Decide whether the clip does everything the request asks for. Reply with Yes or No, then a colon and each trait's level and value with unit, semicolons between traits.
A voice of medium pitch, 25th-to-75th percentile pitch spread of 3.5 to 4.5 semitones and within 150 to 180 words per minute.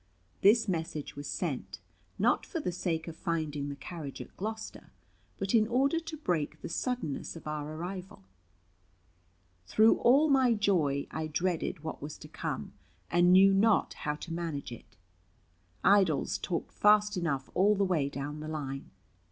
No: medium, 175 Hz; wide, 5.5 semitones; average, 160 wpm